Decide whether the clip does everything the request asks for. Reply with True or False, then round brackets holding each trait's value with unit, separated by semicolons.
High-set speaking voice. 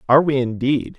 False (135 Hz)